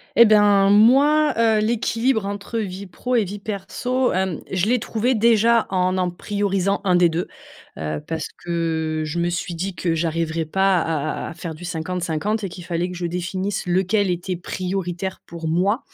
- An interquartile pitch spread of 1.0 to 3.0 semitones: No, average, 3.6 semitones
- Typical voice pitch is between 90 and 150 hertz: No, medium, 185 Hz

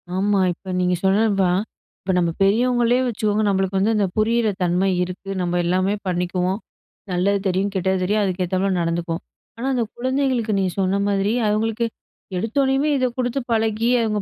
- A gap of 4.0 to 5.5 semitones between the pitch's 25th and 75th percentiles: No, average, 3.5 semitones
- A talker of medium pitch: No, high, 200 Hz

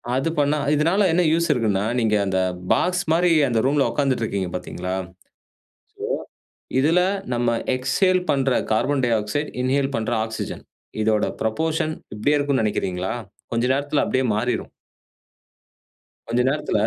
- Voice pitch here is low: Yes, low, 130 Hz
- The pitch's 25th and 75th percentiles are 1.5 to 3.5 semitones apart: No, average, 5.2 semitones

